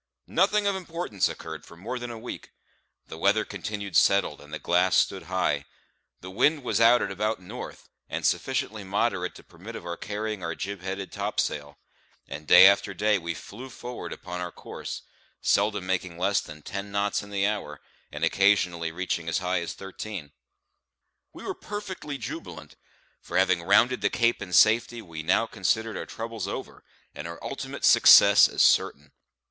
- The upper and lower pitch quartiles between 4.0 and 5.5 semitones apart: No, average, 3.6 semitones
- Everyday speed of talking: Yes, average, 175 wpm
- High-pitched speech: No, low, 100 Hz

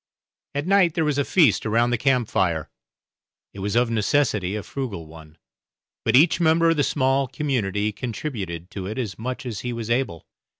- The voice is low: Yes, low, 120 Hz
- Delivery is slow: No, average, 185 wpm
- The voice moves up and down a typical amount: No, wide, 5.9 semitones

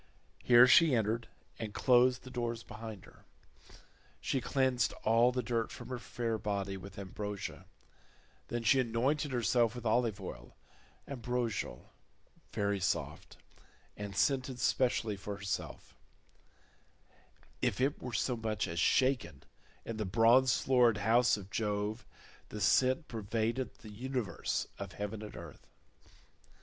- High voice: No, low, 115 Hz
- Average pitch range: Yes, average, 3.3 semitones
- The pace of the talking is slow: Yes, slow, 130 wpm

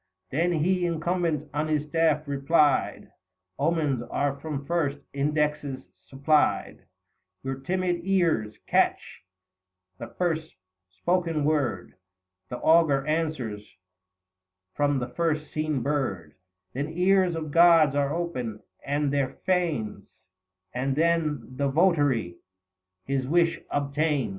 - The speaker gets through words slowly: Yes, slow, 120 wpm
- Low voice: No, medium, 150 Hz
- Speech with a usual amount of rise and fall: Yes, average, 3.5 semitones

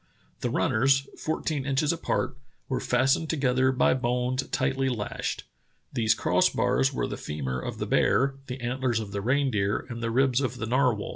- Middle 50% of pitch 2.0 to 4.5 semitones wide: Yes, average, 2.8 semitones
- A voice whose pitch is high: No, low, 130 Hz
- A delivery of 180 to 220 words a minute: No, average, 170 wpm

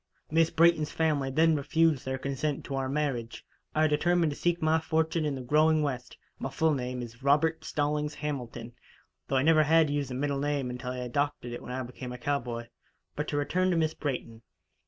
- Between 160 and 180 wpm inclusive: No, average, 200 wpm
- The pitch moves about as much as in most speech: Yes, average, 3.5 semitones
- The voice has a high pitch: No, medium, 145 Hz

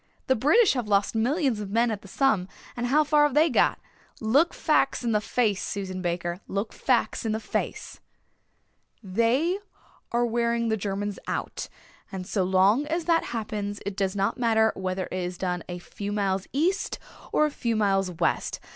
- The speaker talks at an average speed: Yes, average, 180 wpm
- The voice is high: Yes, high, 220 Hz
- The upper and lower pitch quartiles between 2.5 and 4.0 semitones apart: No, average, 4.8 semitones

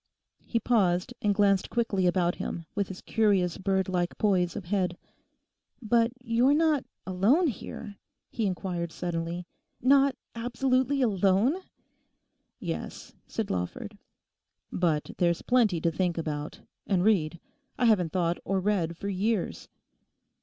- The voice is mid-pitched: No, high, 195 Hz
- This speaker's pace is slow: Yes, slow, 125 wpm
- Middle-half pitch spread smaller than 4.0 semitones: No, average, 4.6 semitones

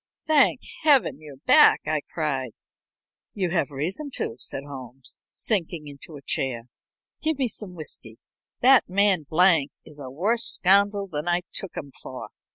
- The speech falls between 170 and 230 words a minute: No, average, 155 wpm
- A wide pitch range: Yes, wide, 6.3 semitones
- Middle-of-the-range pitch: Yes, medium, 165 Hz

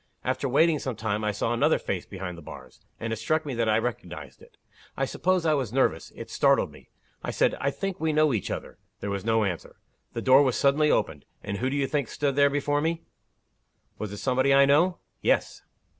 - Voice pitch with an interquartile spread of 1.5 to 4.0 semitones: No, wide, 5.4 semitones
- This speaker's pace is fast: Yes, fast, 220 wpm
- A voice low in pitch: Yes, low, 130 Hz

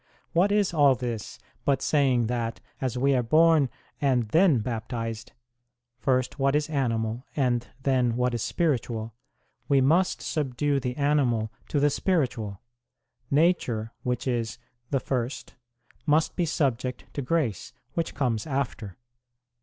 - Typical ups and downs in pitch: Yes, average, 3.9 semitones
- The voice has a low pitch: Yes, low, 130 Hz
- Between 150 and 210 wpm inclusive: No, slow, 135 wpm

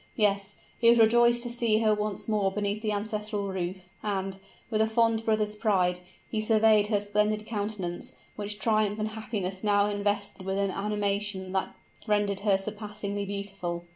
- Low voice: No, high, 210 Hz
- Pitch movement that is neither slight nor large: No, narrow, 1.5 semitones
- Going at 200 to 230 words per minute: No, average, 165 wpm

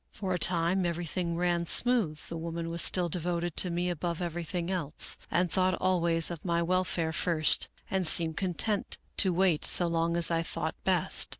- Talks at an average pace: Yes, average, 180 wpm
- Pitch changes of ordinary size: No, narrow, 1.5 semitones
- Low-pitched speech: No, medium, 170 Hz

